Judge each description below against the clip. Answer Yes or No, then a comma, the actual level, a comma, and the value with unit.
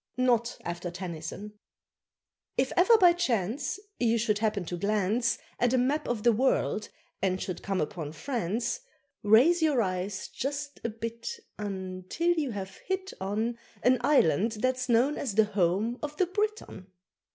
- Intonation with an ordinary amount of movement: No, wide, 5.8 semitones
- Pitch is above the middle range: Yes, high, 230 Hz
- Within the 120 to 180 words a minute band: Yes, average, 160 wpm